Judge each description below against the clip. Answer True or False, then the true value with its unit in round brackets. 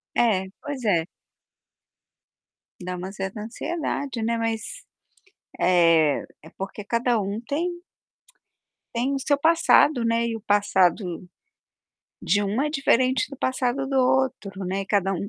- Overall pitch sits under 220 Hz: False (230 Hz)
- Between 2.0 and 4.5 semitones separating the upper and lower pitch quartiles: False (5.4 semitones)